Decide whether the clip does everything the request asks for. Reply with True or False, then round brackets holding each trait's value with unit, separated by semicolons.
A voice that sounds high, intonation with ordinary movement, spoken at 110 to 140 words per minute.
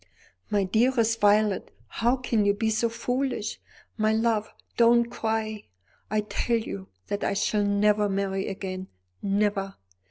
False (215 Hz; 2.2 semitones; 135 wpm)